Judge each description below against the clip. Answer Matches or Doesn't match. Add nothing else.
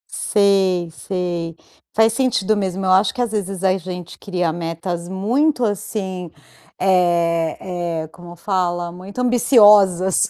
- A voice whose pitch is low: Doesn't match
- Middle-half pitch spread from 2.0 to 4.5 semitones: Matches